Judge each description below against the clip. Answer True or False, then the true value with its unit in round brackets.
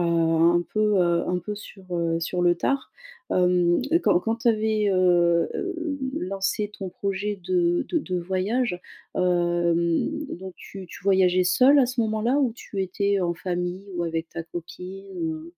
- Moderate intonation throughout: True (3.4 semitones)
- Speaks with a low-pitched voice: False (185 Hz)